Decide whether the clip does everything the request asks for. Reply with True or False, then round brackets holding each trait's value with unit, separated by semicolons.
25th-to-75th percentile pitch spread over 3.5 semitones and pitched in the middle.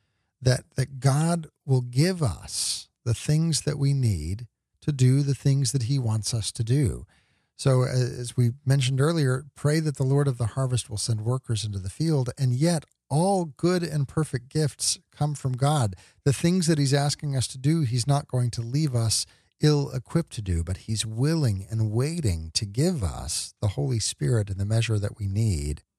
False (4.6 semitones; 130 Hz)